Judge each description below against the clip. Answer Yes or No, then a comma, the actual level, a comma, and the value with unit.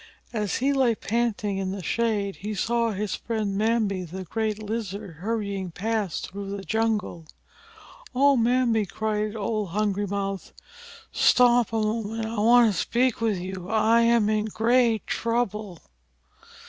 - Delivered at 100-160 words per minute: Yes, average, 145 wpm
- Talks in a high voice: Yes, high, 215 Hz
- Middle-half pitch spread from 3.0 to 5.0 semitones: No, narrow, 2.5 semitones